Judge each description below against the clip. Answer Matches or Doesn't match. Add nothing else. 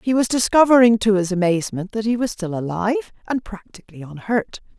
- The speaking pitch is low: Doesn't match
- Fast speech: Doesn't match